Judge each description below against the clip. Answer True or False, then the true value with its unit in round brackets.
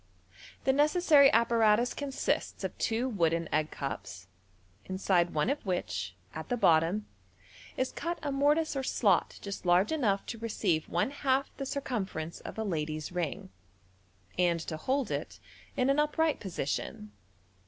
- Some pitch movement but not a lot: False (8.4 semitones)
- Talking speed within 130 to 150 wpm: True (145 wpm)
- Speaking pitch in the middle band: False (210 Hz)